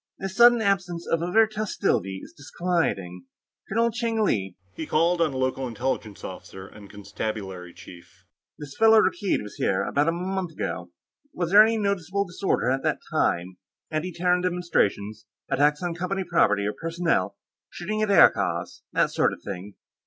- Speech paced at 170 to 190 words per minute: No, average, 160 wpm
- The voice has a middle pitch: Yes, medium, 170 Hz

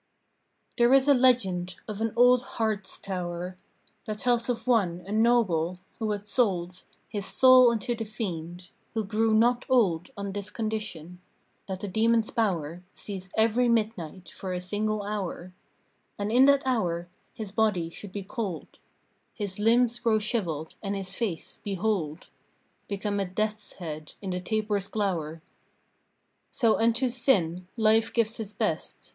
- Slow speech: No, average, 150 wpm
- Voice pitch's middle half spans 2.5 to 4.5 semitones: Yes, average, 3.9 semitones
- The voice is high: Yes, high, 210 Hz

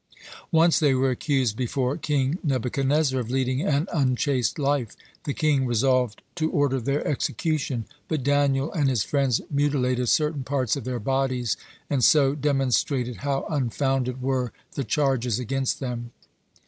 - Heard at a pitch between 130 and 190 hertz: Yes, low, 135 Hz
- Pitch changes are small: Yes, narrow, 2.2 semitones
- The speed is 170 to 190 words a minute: No, average, 145 wpm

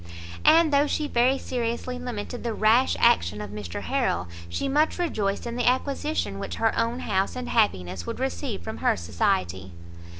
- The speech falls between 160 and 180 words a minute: Yes, average, 170 wpm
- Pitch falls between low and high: No, high, 230 Hz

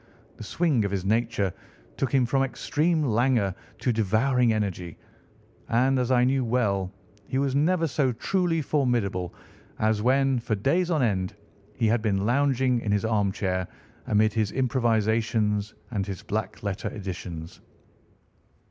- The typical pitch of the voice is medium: No, low, 115 Hz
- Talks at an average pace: Yes, average, 145 wpm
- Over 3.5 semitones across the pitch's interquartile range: Yes, average, 4.5 semitones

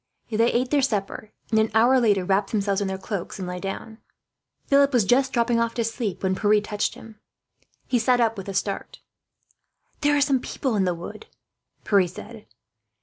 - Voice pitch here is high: Yes, high, 220 Hz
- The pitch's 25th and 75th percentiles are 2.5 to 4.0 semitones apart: Yes, average, 3.7 semitones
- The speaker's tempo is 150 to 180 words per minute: No, average, 195 wpm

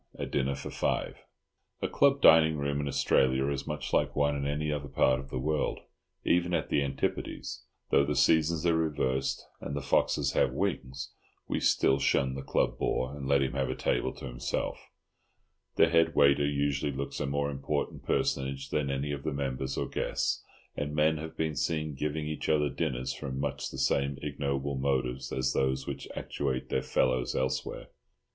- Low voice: Yes, very low, 70 Hz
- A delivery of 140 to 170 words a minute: No, average, 180 wpm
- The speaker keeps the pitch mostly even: Yes, narrow, 1.9 semitones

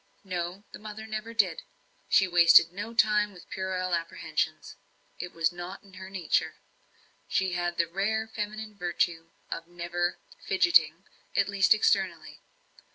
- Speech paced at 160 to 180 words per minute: No, slow, 135 wpm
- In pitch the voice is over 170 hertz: Yes, medium, 185 Hz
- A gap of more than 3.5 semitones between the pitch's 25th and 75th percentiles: No, average, 3.1 semitones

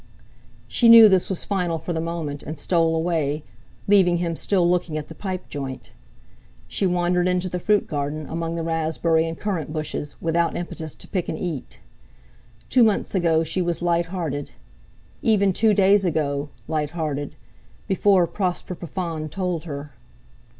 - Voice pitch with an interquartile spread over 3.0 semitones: No, average, 2.7 semitones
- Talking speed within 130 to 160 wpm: Yes, average, 155 wpm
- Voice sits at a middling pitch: Yes, medium, 170 Hz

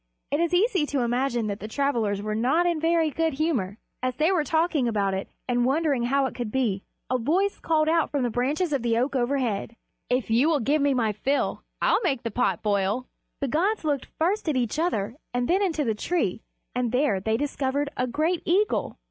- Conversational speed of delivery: No, fast, 215 wpm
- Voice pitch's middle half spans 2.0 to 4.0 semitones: No, average, 5.3 semitones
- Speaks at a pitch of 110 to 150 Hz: No, very high, 270 Hz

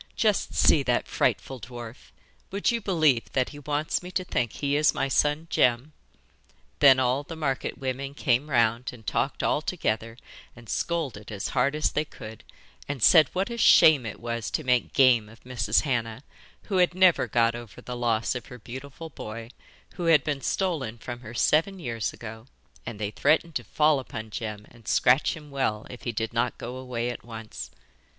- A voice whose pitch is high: No, low, 125 Hz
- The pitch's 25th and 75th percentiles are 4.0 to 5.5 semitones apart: Yes, average, 4.5 semitones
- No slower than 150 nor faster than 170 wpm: No, average, 190 wpm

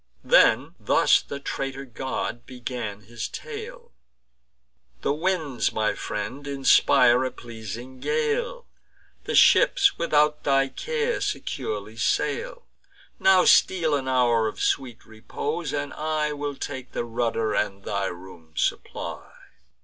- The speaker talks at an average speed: No, slow, 120 wpm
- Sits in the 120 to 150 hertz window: Yes, low, 135 Hz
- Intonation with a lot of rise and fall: Yes, wide, 6.3 semitones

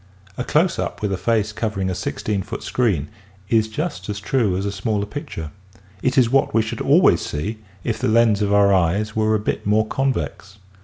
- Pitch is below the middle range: Yes, low, 105 Hz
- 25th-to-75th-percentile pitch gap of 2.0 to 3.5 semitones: Yes, narrow, 2.5 semitones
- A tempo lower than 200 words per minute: No, fast, 205 wpm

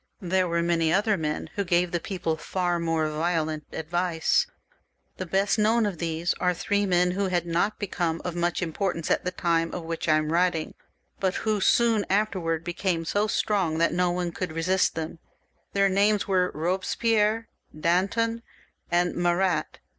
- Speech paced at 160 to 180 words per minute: Yes, average, 170 wpm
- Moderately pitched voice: Yes, medium, 180 Hz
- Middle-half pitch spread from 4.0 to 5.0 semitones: No, average, 2.9 semitones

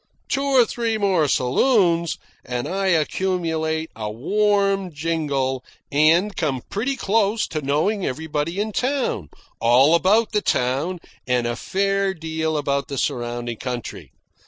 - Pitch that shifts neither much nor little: No, wide, 6.4 semitones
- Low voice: No, medium, 165 Hz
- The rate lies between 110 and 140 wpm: Yes, slow, 135 wpm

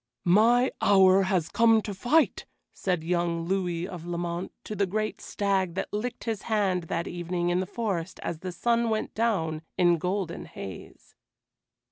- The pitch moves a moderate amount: Yes, average, 3.7 semitones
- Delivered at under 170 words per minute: Yes, average, 160 wpm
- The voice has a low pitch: No, medium, 185 Hz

